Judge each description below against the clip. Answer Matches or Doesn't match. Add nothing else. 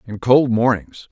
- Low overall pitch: Matches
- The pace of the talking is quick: Doesn't match